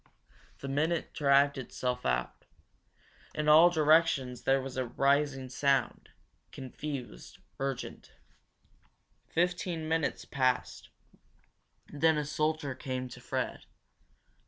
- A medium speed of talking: No, slow, 100 wpm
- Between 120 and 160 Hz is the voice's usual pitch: Yes, medium, 140 Hz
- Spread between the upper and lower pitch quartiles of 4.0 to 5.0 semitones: No, average, 3.1 semitones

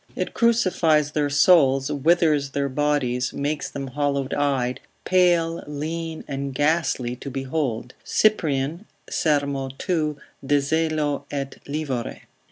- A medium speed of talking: No, slow, 115 wpm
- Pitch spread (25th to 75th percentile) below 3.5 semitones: Yes, average, 2.7 semitones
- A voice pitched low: No, medium, 145 Hz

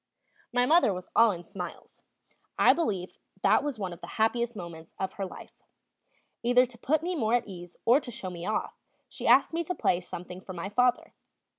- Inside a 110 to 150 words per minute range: No, average, 200 wpm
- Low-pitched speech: No, high, 220 Hz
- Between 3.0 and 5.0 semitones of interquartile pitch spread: No, wide, 5.6 semitones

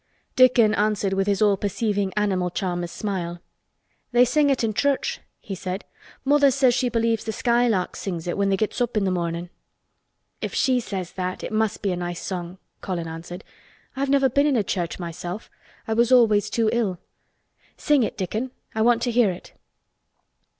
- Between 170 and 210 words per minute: Yes, average, 185 wpm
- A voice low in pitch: No, high, 210 Hz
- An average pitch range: Yes, average, 4.8 semitones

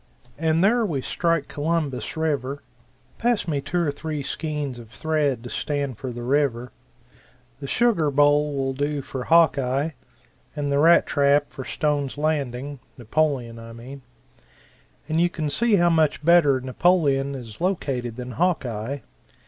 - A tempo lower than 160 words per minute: Yes, average, 150 wpm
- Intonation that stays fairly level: No, average, 3.4 semitones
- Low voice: No, medium, 145 Hz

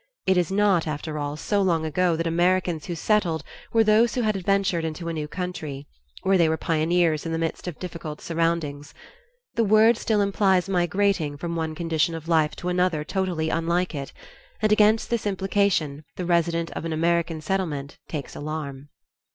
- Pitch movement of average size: Yes, average, 3.2 semitones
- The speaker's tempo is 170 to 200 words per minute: Yes, average, 180 wpm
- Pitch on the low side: No, medium, 170 Hz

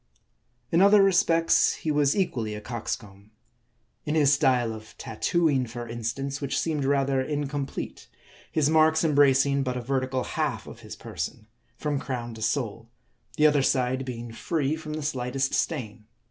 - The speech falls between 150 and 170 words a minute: Yes, average, 155 wpm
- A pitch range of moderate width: Yes, average, 3.8 semitones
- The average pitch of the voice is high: No, low, 135 Hz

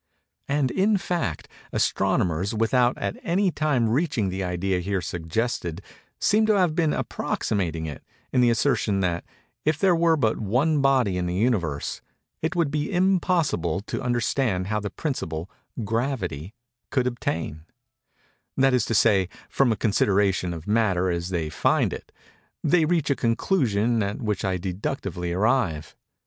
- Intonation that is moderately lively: No, wide, 7.2 semitones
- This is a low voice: Yes, low, 110 Hz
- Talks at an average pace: Yes, average, 150 wpm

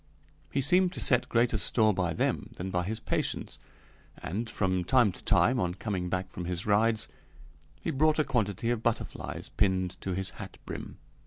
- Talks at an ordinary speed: Yes, average, 180 wpm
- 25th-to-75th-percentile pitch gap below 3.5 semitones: No, average, 4.6 semitones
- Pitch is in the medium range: No, low, 105 Hz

